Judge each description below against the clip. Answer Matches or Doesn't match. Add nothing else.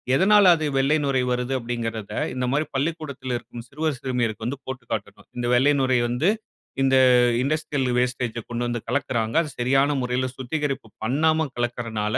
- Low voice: Matches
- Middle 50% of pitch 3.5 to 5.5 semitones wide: Doesn't match